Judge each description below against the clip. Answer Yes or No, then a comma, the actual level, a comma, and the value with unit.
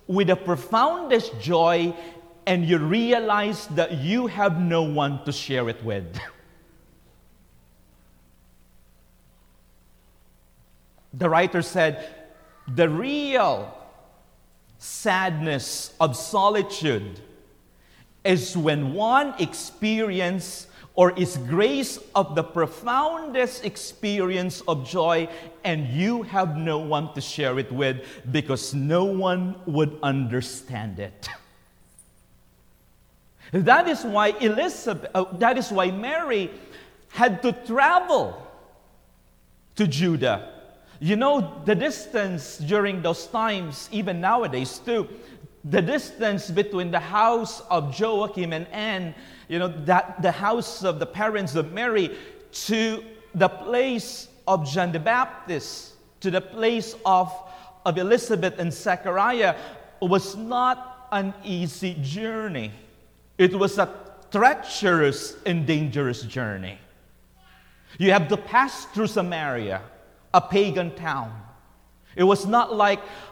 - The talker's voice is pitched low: No, medium, 180 Hz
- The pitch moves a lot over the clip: Yes, wide, 6.5 semitones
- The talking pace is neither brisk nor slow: No, slow, 110 wpm